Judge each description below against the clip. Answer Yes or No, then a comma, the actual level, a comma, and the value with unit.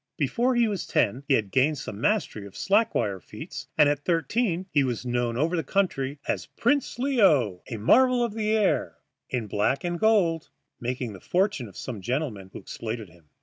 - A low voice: No, medium, 145 Hz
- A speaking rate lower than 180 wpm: No, average, 190 wpm